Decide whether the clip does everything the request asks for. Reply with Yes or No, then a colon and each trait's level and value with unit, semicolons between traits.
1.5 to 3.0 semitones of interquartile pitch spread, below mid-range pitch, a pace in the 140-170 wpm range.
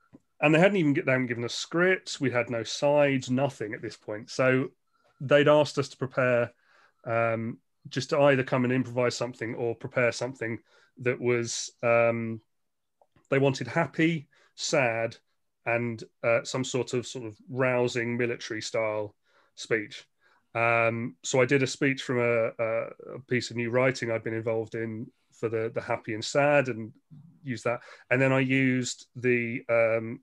Yes: average, 2.7 semitones; low, 125 Hz; average, 165 wpm